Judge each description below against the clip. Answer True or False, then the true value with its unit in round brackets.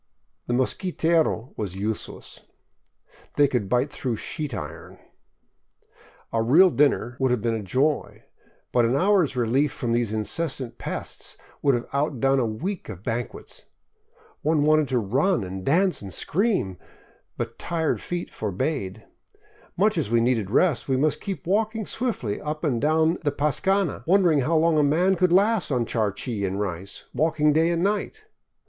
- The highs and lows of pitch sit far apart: True (6.4 semitones)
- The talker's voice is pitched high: False (140 Hz)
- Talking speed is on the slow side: False (155 wpm)